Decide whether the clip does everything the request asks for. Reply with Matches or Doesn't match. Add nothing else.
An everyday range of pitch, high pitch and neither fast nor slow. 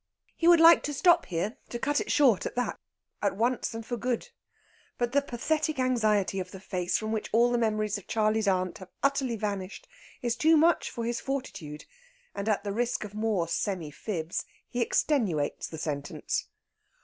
Matches